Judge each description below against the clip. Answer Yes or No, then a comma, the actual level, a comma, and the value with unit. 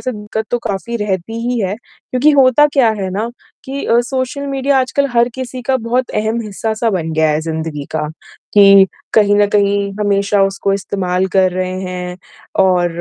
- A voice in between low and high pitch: No, high, 205 Hz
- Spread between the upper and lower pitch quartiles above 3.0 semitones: Yes, average, 4.5 semitones